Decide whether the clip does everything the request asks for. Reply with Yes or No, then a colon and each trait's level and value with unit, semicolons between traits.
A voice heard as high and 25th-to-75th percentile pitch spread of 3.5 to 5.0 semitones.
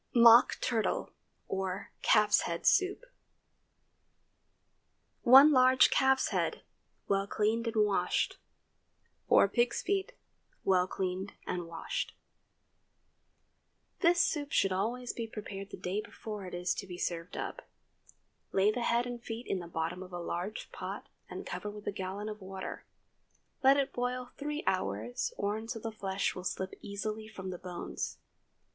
Yes: high, 210 Hz; average, 4.6 semitones